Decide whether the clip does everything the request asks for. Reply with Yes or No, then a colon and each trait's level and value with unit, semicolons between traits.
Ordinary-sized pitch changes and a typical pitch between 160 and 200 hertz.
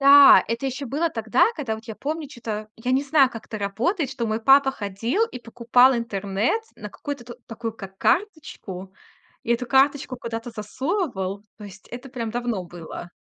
No: average, 4.1 semitones; high, 235 Hz